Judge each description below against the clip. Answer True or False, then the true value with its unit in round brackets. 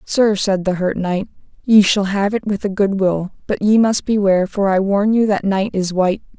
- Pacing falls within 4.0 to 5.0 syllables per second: True (4.8 syllables/s)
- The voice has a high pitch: True (200 Hz)